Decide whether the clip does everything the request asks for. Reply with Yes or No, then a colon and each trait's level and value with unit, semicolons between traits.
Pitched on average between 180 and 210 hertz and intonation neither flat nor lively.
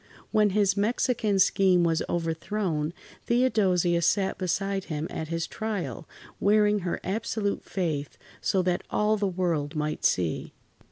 Yes: medium, 185 Hz; average, 3.8 semitones